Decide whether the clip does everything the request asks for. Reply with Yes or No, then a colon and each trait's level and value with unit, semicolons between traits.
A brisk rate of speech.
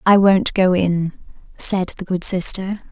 No: average, 165 wpm